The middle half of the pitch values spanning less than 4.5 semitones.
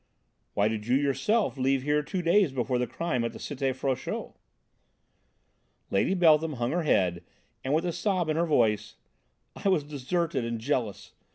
No: wide, 5.5 semitones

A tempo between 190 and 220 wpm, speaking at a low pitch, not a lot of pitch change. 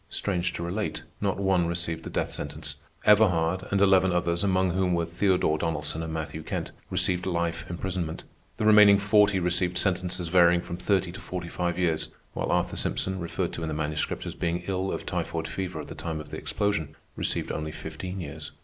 Yes: average, 195 wpm; very low, 90 Hz; narrow, 2.3 semitones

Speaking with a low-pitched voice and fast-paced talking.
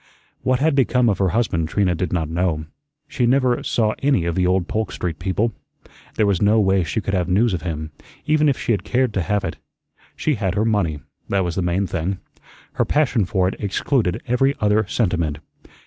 Yes: low, 100 Hz; fast, 210 wpm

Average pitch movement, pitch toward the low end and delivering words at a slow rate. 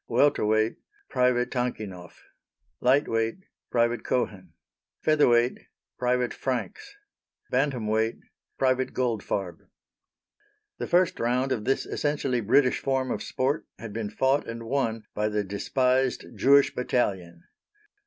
Yes: average, 3.3 semitones; low, 125 Hz; slow, 120 wpm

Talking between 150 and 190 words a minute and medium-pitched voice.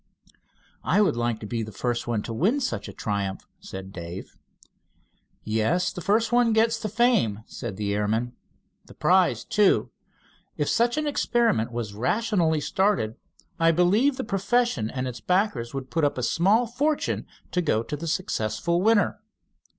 Yes: average, 165 wpm; medium, 165 Hz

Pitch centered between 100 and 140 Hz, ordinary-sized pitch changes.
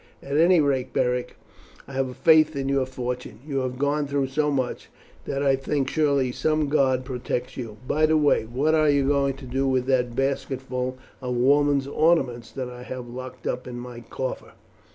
No: low, 135 Hz; narrow, 2.2 semitones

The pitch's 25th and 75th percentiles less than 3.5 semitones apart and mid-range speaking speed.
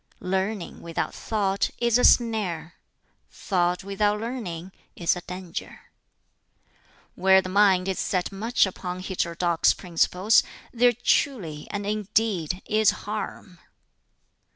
No: average, 3.1 semitones; slow, 110 wpm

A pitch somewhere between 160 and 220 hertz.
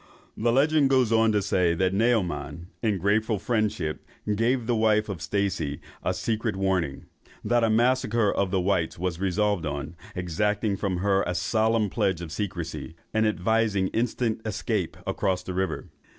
No: low, 100 Hz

